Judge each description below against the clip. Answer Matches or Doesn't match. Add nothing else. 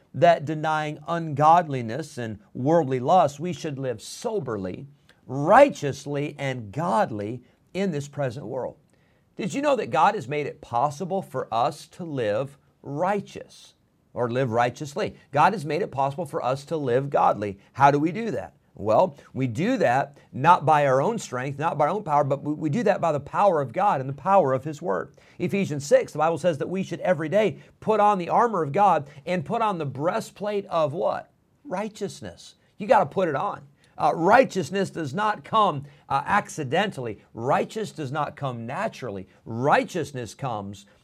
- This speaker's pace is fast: Doesn't match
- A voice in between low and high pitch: Matches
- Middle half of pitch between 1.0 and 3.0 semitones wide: Doesn't match